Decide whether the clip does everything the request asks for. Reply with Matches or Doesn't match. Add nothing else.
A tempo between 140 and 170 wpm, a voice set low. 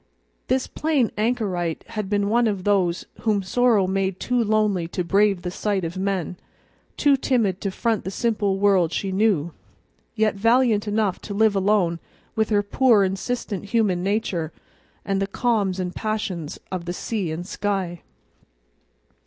Doesn't match